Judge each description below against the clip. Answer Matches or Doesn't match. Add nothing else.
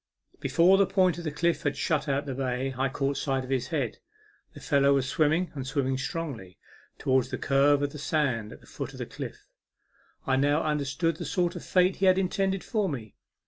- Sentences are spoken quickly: Matches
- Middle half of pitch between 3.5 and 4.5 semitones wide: Matches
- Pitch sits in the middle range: Matches